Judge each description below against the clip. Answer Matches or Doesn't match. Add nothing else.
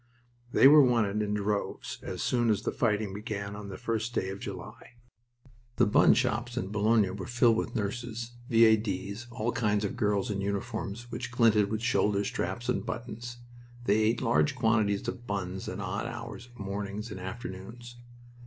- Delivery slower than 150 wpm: Doesn't match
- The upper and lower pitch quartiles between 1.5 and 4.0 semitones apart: Matches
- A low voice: Matches